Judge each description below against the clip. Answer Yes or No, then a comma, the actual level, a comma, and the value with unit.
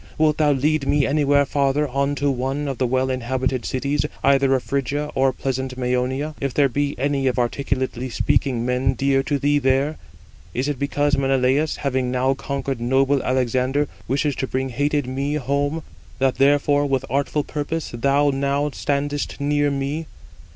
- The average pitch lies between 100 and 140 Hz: Yes, low, 135 Hz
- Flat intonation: Yes, narrow, 1.7 semitones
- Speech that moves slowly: No, average, 165 wpm